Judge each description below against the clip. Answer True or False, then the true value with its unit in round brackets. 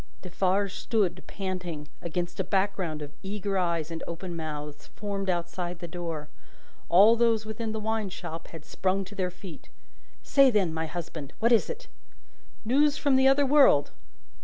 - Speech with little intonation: False (4.3 semitones)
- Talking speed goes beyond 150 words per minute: True (160 wpm)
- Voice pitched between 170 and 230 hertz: True (185 Hz)